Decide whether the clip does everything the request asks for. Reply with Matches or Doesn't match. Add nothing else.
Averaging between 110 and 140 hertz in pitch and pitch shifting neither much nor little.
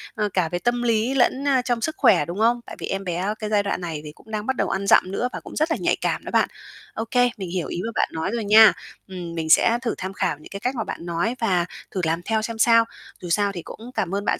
Doesn't match